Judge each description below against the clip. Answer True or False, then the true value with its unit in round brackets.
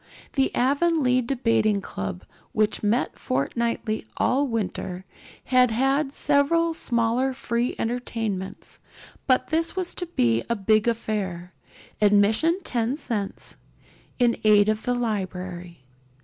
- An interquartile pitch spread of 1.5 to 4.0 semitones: False (4.6 semitones)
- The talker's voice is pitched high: True (230 Hz)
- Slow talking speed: True (115 wpm)